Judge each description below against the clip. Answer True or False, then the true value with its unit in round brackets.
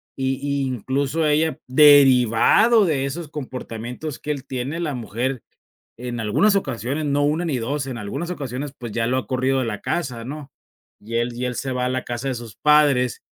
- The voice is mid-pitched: False (130 Hz)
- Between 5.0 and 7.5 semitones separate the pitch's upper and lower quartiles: False (3.3 semitones)